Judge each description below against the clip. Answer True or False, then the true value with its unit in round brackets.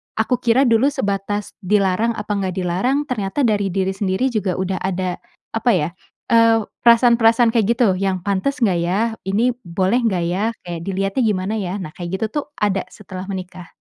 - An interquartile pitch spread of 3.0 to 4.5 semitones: True (3.5 semitones)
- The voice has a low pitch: False (200 Hz)